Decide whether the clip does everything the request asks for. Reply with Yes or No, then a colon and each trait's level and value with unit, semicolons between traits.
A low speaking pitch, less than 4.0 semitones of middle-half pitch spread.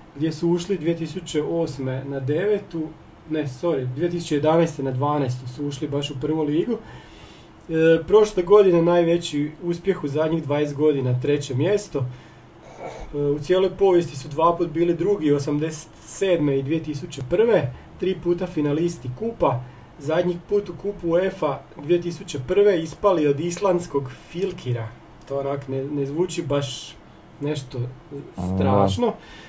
No: medium, 155 Hz; average, 3.6 semitones